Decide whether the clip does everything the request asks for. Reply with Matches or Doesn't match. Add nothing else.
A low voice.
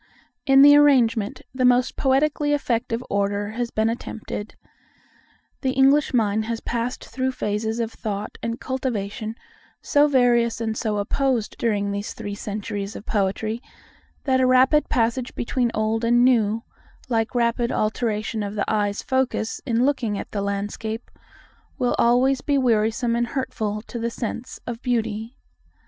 Doesn't match